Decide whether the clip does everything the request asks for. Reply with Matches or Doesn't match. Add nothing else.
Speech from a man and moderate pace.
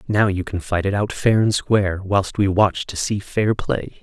Doesn't match